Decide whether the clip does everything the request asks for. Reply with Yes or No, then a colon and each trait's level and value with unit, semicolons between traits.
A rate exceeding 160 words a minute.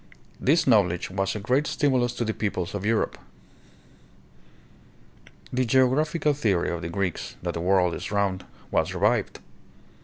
No: average, 150 wpm